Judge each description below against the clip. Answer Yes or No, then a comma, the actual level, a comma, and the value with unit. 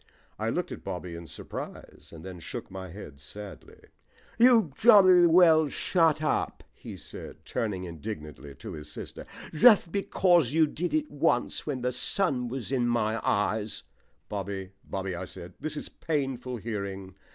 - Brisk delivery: No, average, 160 wpm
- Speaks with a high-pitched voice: No, low, 120 Hz